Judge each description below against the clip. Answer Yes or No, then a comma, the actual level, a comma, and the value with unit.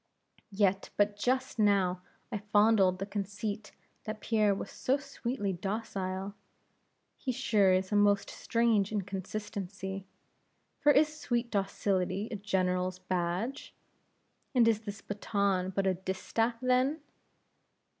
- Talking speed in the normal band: No, slow, 120 wpm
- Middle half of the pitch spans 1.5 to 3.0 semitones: Yes, average, 2.7 semitones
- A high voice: Yes, high, 205 Hz